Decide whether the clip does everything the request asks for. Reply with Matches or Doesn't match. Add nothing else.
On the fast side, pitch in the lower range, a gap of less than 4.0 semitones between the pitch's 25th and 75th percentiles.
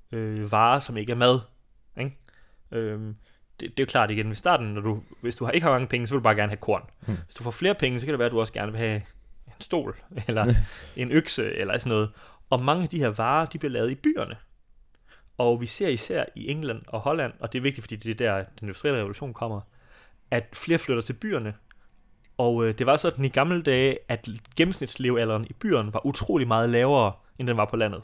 Matches